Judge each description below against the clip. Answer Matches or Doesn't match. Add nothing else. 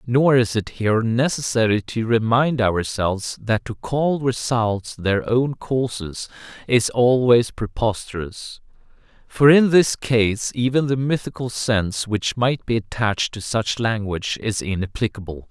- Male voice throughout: Matches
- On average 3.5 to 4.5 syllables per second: Matches